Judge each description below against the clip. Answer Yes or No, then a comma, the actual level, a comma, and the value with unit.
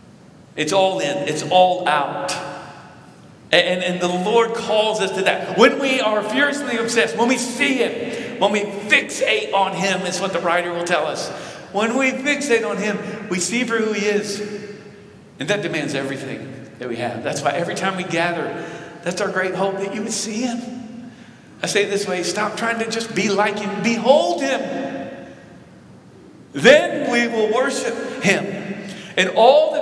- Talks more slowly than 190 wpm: Yes, average, 180 wpm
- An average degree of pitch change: Yes, average, 4.2 semitones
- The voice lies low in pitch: No, high, 205 Hz